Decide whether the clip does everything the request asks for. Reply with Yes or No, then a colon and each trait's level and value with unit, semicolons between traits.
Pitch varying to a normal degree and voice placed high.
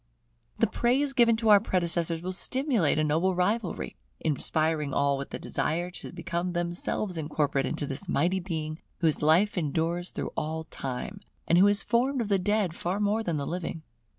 No: average, 4.5 semitones; medium, 175 Hz